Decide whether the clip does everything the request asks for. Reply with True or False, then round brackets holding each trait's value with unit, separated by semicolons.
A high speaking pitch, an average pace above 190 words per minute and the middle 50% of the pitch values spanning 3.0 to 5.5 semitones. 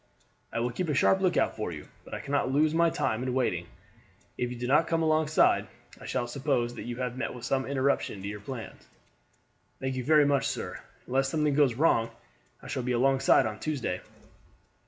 False (130 Hz; 200 wpm; 3.6 semitones)